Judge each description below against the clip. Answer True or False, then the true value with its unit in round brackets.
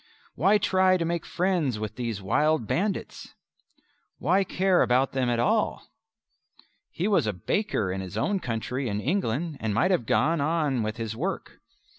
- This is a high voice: False (140 Hz)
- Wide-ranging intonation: True (8.5 semitones)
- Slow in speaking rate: False (165 wpm)